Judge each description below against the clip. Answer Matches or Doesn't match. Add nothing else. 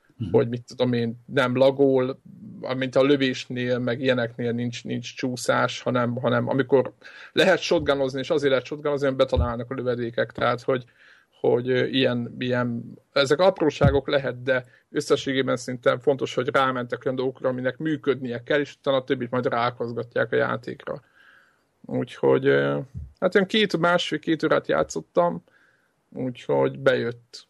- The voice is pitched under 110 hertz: Doesn't match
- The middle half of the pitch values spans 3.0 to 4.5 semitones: Doesn't match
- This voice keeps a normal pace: Matches